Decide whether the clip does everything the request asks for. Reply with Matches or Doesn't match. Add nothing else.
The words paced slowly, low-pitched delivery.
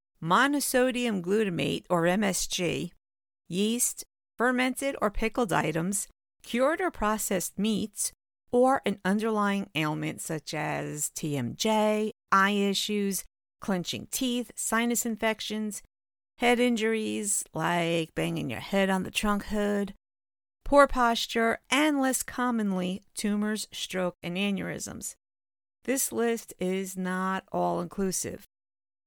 Doesn't match